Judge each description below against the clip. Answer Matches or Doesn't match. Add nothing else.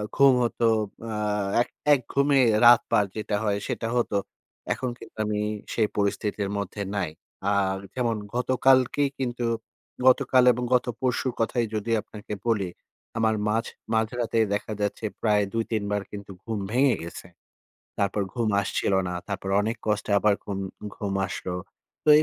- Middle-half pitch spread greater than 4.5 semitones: Doesn't match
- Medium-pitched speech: Doesn't match